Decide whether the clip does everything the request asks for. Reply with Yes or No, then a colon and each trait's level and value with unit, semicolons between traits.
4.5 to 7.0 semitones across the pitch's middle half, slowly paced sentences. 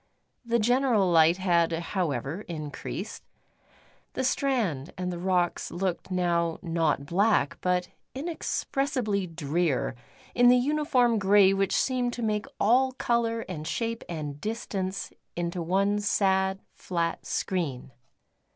Yes: average, 5.2 semitones; slow, 120 wpm